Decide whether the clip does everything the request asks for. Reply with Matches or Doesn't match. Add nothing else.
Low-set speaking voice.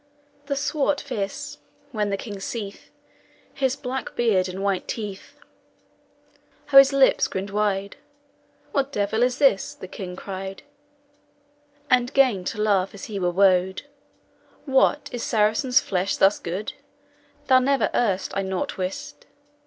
Doesn't match